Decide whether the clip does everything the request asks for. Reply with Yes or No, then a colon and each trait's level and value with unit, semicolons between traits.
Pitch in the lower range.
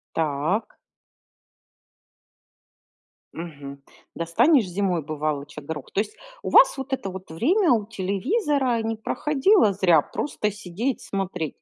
No: high, 195 Hz